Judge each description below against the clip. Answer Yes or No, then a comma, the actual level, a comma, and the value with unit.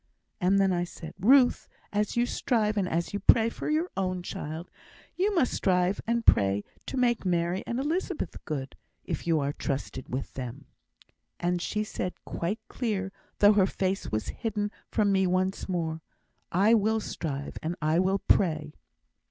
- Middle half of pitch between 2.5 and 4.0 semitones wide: No, average, 4.6 semitones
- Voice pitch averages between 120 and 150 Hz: No, high, 190 Hz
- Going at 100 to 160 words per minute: No, average, 175 wpm